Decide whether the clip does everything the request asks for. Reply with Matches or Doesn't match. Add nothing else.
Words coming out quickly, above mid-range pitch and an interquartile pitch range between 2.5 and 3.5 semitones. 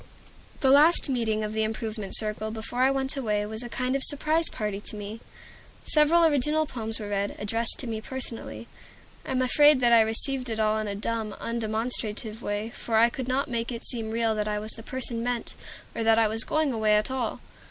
Matches